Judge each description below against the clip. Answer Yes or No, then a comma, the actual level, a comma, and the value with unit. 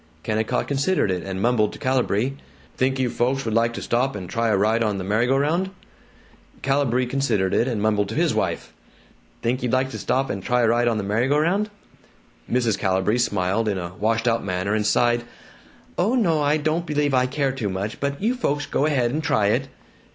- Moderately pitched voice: No, low, 120 Hz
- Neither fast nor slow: No, fast, 215 wpm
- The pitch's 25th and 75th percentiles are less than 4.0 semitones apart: No, average, 4.6 semitones